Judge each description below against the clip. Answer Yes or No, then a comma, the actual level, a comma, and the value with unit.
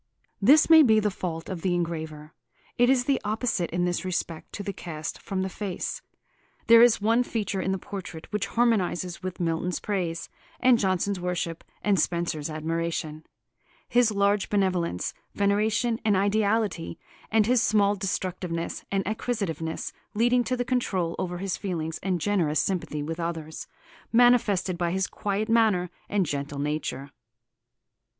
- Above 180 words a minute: No, average, 150 wpm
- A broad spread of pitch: No, average, 4.3 semitones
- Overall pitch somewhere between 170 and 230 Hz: Yes, high, 190 Hz